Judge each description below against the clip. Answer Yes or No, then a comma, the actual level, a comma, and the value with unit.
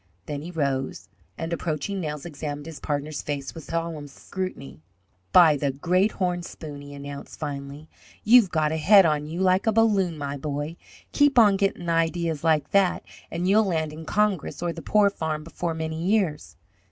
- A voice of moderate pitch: Yes, medium, 165 Hz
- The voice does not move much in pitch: No, average, 3.8 semitones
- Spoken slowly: No, average, 175 wpm